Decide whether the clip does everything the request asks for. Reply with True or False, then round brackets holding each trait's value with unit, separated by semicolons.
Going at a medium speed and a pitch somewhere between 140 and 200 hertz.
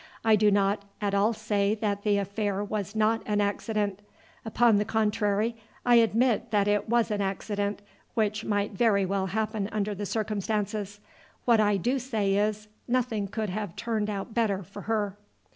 False (170 wpm; 210 Hz)